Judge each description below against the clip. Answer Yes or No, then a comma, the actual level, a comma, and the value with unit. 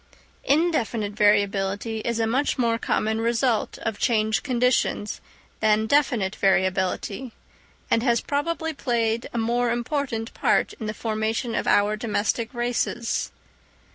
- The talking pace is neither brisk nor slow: No, slow, 130 wpm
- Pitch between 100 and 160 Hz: No, high, 230 Hz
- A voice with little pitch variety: Yes, narrow, 2.2 semitones